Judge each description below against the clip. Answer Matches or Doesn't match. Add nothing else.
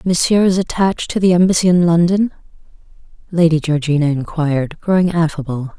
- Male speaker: Doesn't match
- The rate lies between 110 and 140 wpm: Matches